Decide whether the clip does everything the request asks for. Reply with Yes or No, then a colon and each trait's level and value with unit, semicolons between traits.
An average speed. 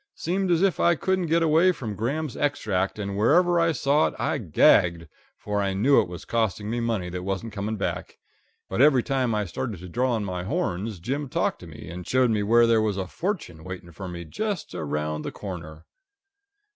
No: fast, 210 wpm